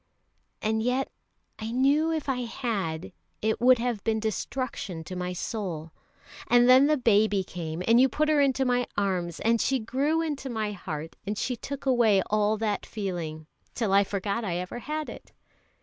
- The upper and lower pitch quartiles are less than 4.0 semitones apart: No, average, 4.8 semitones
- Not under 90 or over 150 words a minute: No, average, 180 wpm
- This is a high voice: Yes, high, 220 Hz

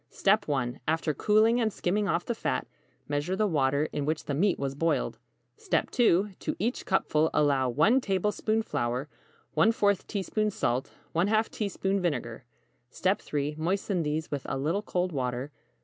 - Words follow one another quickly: No, average, 150 wpm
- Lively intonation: Yes, wide, 6.1 semitones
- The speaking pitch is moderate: Yes, medium, 170 Hz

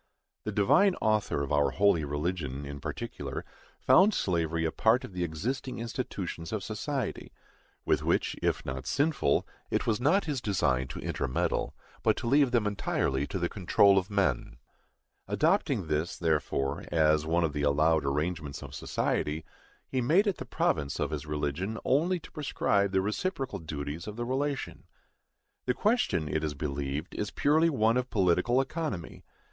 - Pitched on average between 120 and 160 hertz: No, very low, 95 Hz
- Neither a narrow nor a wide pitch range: No, wide, 8.8 semitones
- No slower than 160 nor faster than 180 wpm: Yes, average, 165 wpm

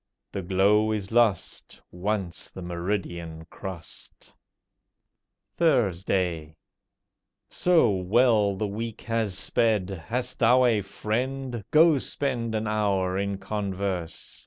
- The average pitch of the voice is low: Yes, low, 105 Hz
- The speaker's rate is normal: No, slow, 105 wpm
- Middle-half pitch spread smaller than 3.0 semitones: No, average, 3.7 semitones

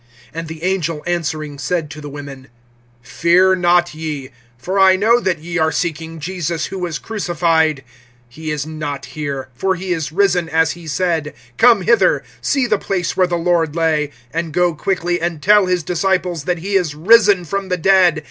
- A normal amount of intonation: Yes, average, 3.0 semitones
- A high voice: No, medium, 170 Hz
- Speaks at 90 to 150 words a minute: No, average, 185 wpm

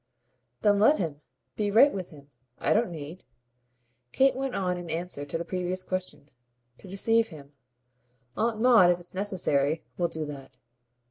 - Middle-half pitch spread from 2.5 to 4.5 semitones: No, average, 4.9 semitones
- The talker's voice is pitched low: No, medium, 180 Hz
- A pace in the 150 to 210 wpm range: Yes, average, 160 wpm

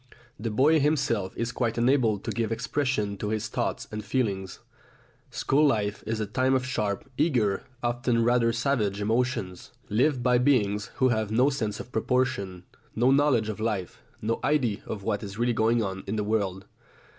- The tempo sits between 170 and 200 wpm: Yes, average, 175 wpm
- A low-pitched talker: Yes, low, 115 Hz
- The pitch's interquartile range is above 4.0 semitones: No, average, 3.6 semitones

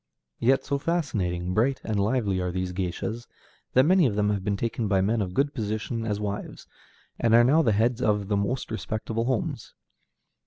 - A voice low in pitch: Yes, low, 110 Hz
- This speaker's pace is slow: No, average, 190 wpm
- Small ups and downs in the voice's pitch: No, average, 3.6 semitones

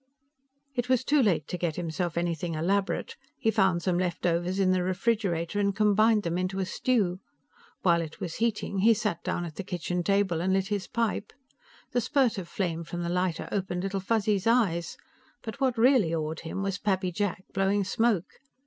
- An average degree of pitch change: Yes, average, 3.4 semitones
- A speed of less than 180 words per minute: No, average, 185 wpm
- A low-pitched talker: No, high, 190 Hz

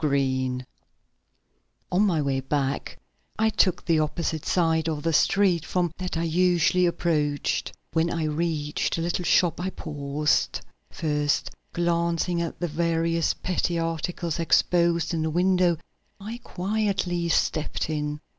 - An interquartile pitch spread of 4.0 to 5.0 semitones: No, narrow, 2.6 semitones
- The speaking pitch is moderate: Yes, medium, 165 Hz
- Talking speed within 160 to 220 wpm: No, slow, 135 wpm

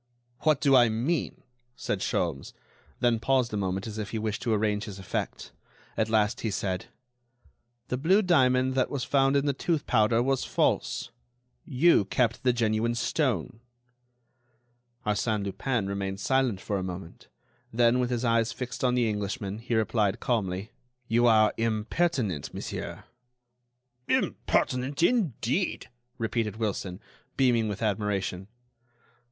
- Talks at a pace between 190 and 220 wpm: No, average, 140 wpm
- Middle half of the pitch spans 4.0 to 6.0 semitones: No, average, 3.6 semitones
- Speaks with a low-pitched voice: Yes, low, 115 Hz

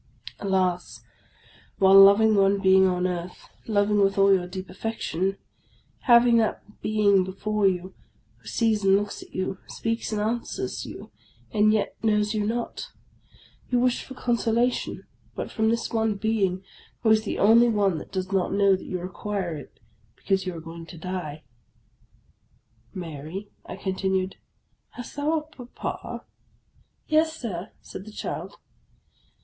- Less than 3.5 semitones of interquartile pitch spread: Yes, average, 2.9 semitones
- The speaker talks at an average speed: Yes, average, 155 wpm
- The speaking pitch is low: No, high, 200 Hz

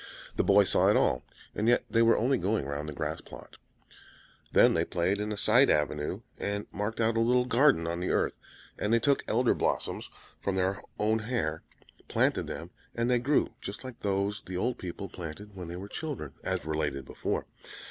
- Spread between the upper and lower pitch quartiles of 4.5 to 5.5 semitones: Yes, average, 5.1 semitones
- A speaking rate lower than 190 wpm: No, average, 195 wpm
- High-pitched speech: No, low, 100 Hz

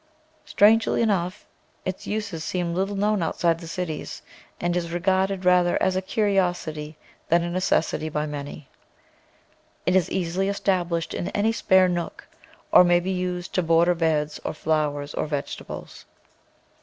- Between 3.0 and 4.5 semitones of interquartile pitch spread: No, narrow, 2.4 semitones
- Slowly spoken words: No, average, 150 wpm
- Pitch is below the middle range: No, medium, 175 Hz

